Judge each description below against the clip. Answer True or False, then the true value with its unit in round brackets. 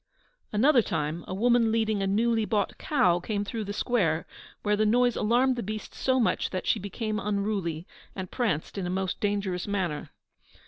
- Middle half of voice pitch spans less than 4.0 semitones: True (3.4 semitones)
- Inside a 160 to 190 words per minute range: True (180 wpm)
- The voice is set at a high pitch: True (210 Hz)